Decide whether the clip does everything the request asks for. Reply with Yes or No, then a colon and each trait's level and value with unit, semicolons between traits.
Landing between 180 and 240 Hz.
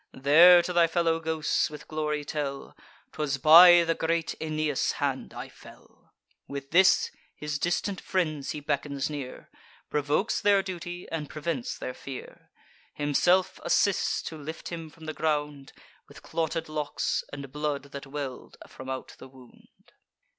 No: medium, 155 Hz